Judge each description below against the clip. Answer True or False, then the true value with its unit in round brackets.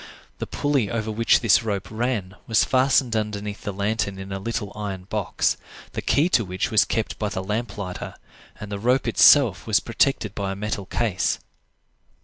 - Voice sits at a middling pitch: False (105 Hz)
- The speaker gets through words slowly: False (180 wpm)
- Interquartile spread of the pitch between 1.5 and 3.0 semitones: True (2.7 semitones)